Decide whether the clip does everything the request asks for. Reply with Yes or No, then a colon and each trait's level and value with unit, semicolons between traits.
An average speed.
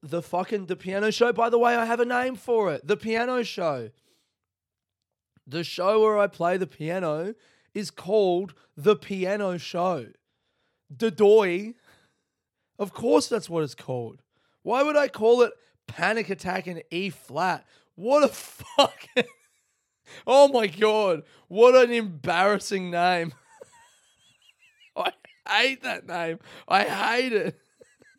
No: slow, 130 wpm